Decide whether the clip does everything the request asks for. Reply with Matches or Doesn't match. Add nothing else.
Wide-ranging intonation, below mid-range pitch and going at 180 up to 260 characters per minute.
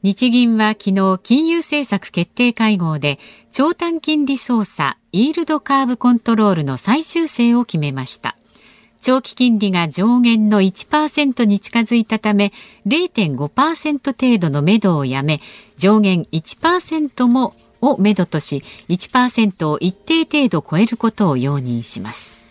Doesn't match